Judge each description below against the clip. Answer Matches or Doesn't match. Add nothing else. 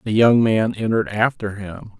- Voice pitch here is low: Matches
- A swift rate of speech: Doesn't match